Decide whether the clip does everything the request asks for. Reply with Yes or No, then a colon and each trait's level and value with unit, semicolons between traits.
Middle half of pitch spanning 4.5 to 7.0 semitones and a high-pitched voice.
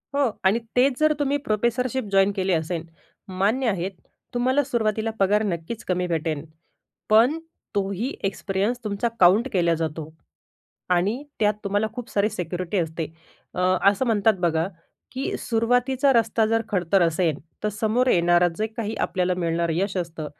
Yes: average, 4.8 semitones; high, 200 Hz